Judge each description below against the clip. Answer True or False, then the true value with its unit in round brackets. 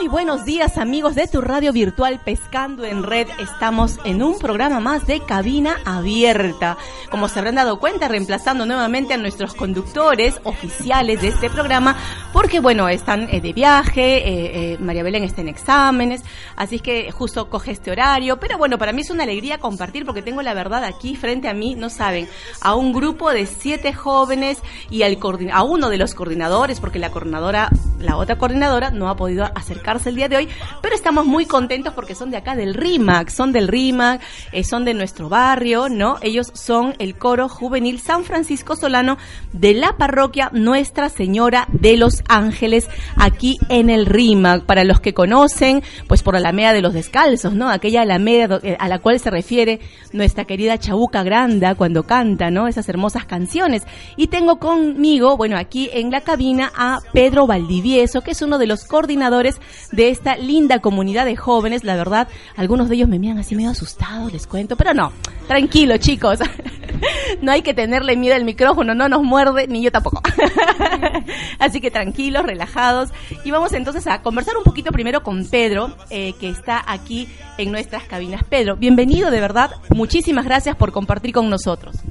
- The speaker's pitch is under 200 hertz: False (240 Hz)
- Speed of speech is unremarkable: True (180 wpm)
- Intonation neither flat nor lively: True (4.7 semitones)